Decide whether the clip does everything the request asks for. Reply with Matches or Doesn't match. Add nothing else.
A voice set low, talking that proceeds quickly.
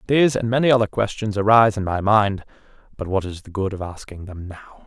Matches